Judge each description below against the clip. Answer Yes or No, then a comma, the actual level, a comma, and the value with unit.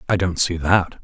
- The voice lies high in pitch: No, very low, 90 Hz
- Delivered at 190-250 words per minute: Yes, fast, 235 wpm